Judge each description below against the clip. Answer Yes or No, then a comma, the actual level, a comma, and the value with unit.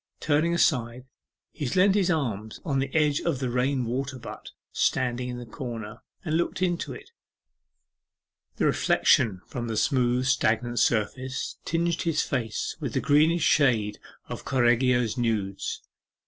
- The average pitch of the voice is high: No, low, 125 Hz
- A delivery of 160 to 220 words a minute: No, average, 145 wpm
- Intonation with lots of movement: No, average, 4.0 semitones